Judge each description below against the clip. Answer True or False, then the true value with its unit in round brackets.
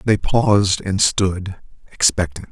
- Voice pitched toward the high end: False (95 Hz)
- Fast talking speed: False (120 wpm)